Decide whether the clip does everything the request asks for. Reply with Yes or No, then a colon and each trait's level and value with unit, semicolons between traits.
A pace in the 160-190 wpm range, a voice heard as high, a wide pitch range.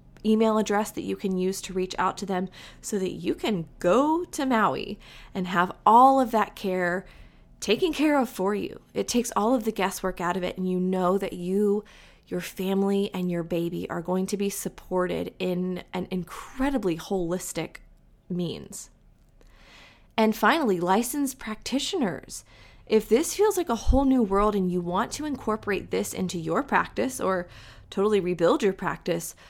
No: average, 170 wpm; high, 195 Hz; average, 3.4 semitones